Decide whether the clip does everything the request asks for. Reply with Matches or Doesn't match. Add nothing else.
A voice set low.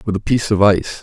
Matches